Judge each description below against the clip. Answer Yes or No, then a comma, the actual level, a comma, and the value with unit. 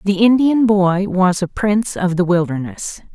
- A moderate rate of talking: Yes, average, 170 wpm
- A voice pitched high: Yes, high, 195 Hz